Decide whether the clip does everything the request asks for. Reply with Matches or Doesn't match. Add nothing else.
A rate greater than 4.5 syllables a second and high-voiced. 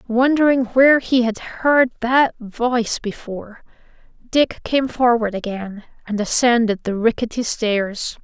Doesn't match